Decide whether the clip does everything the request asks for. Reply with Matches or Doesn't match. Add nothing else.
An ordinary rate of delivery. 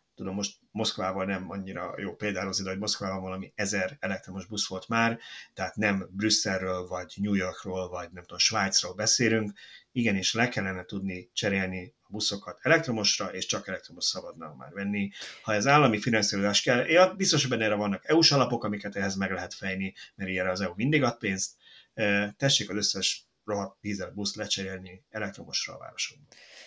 Doesn't match